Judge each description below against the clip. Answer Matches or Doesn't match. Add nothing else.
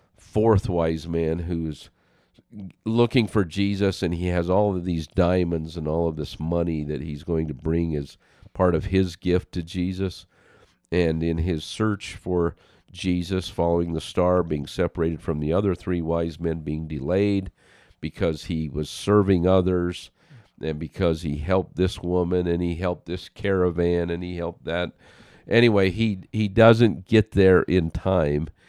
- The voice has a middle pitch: Doesn't match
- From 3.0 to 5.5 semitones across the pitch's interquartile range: Doesn't match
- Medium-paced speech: Matches